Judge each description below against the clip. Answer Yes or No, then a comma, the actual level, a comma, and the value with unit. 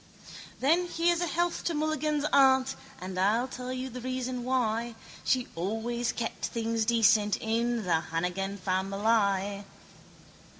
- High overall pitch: Yes, high, 235 Hz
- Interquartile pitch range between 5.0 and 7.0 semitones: No, average, 4.4 semitones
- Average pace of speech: No, slow, 130 wpm